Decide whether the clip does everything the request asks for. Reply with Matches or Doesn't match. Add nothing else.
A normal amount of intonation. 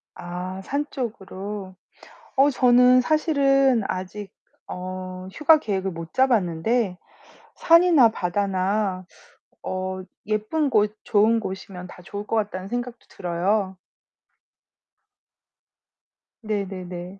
Matches